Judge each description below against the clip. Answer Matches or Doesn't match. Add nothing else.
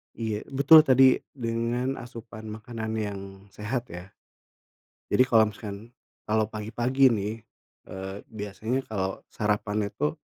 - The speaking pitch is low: Matches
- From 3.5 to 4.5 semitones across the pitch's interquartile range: Doesn't match